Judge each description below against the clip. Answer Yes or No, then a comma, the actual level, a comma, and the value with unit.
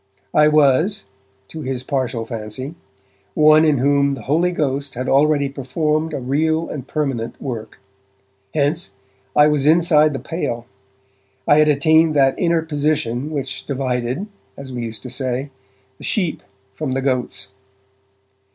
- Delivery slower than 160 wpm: Yes, average, 140 wpm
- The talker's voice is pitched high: No, medium, 140 Hz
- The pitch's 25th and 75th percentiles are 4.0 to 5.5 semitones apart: No, average, 3.1 semitones